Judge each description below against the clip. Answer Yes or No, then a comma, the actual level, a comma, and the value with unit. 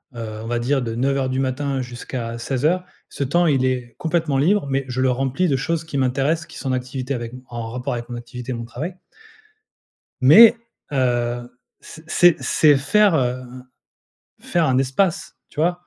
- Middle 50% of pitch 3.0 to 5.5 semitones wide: Yes, average, 3.6 semitones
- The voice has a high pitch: No, low, 130 Hz